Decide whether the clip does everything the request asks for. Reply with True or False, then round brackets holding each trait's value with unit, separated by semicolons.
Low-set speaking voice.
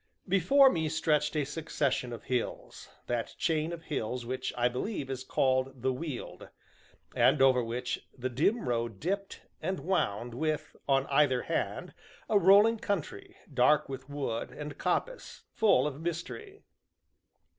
False (145 Hz)